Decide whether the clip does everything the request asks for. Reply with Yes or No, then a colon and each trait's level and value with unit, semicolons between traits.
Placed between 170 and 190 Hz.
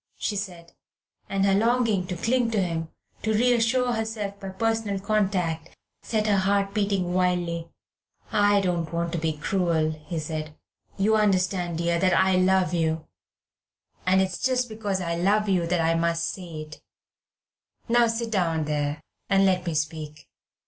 Yes: medium, 185 Hz